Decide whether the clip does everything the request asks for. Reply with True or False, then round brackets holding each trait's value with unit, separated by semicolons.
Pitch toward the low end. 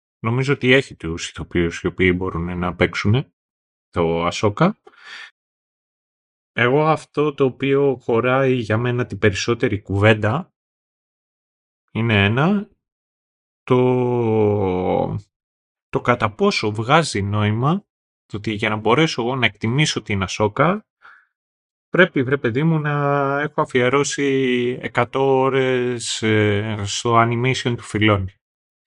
True (120 Hz)